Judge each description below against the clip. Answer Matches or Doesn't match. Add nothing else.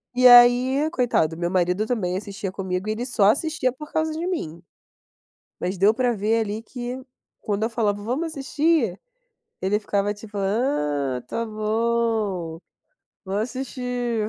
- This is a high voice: Matches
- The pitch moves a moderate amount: Matches